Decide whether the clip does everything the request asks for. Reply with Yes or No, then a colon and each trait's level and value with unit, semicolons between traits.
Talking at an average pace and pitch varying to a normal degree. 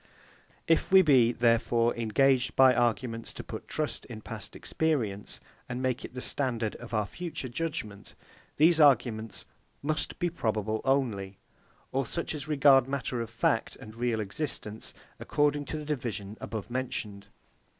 Yes: average, 150 wpm; average, 4.3 semitones